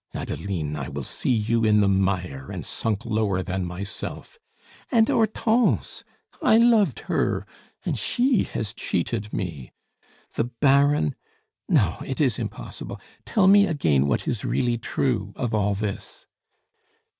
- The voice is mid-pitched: No, low, 110 Hz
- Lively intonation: Yes, wide, 7.2 semitones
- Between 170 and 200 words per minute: No, slow, 135 wpm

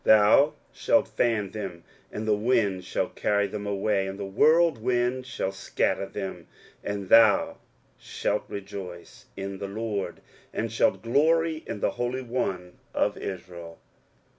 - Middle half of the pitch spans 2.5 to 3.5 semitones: No, average, 3.9 semitones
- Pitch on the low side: Yes, low, 105 Hz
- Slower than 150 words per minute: Yes, average, 140 wpm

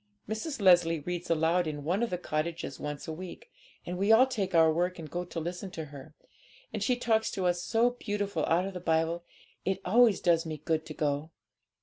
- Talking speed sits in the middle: No, fast, 215 wpm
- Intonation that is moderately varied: Yes, average, 3.5 semitones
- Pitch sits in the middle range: Yes, medium, 175 Hz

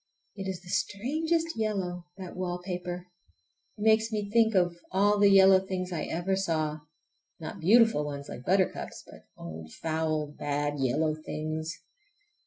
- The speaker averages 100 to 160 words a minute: Yes, average, 140 wpm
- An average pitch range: Yes, average, 4.3 semitones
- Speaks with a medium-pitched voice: Yes, medium, 180 Hz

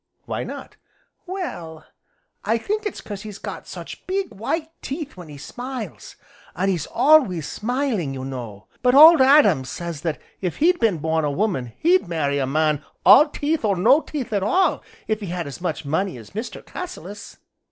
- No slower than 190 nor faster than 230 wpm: No, average, 180 wpm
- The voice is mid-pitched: No, high, 200 Hz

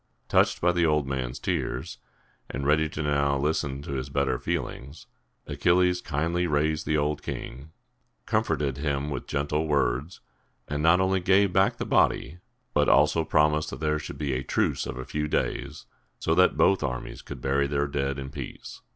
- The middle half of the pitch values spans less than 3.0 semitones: Yes, narrow, 2.6 semitones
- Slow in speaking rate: No, average, 175 wpm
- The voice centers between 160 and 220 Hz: No, very low, 75 Hz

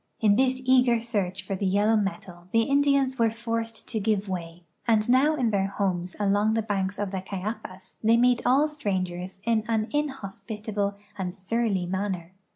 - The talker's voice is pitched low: No, high, 210 Hz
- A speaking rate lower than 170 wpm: No, average, 175 wpm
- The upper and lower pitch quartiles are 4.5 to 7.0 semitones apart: No, average, 3.4 semitones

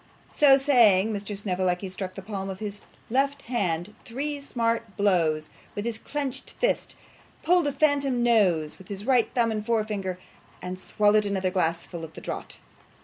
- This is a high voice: Yes, high, 210 Hz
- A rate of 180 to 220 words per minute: No, average, 160 wpm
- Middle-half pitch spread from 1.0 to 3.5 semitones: No, average, 4.8 semitones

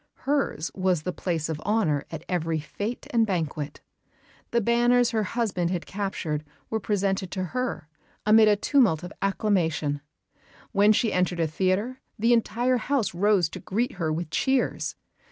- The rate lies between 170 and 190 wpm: No, average, 155 wpm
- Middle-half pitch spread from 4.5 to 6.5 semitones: Yes, wide, 5.4 semitones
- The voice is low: No, high, 195 Hz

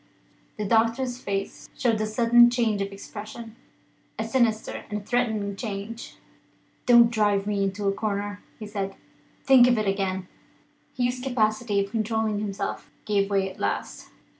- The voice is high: Yes, high, 215 Hz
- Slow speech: No, average, 145 wpm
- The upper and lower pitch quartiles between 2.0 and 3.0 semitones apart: Yes, average, 2.7 semitones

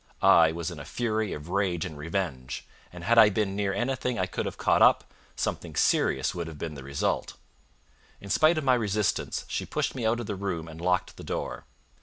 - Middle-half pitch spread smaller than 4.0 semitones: No, average, 5.0 semitones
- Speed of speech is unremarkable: No, fast, 215 wpm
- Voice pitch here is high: No, very low, 95 Hz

